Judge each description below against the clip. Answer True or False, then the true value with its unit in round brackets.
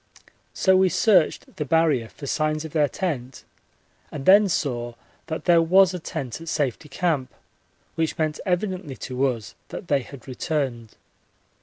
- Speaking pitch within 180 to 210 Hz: False (155 Hz)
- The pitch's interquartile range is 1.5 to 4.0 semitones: False (4.8 semitones)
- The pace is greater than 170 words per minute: False (155 wpm)